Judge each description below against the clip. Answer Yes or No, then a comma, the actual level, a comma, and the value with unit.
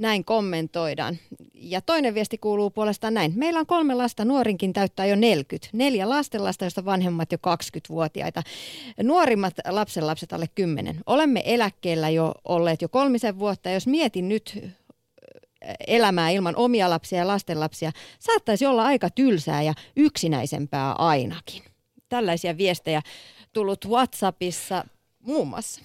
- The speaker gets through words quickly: No, average, 130 wpm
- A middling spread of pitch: No, wide, 5.8 semitones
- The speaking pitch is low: No, high, 195 Hz